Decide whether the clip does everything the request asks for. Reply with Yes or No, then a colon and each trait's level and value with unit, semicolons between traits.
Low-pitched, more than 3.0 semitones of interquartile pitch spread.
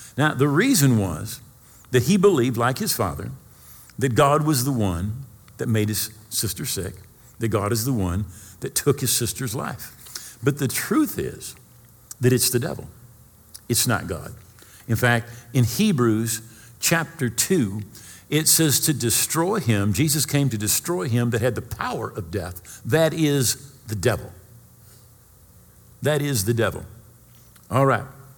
Yes: low, 120 Hz; average, 3.7 semitones